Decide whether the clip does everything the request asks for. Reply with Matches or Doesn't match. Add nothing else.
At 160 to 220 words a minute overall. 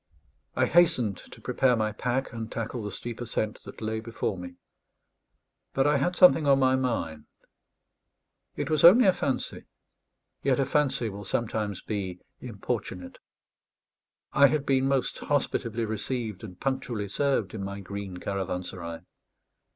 Doesn't match